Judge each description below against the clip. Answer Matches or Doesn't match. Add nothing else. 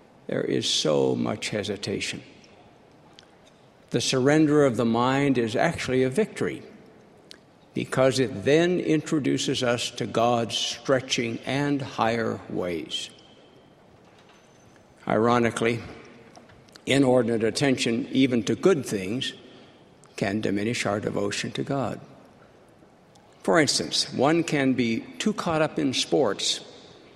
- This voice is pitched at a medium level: Doesn't match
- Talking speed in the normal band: Doesn't match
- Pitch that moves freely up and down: Doesn't match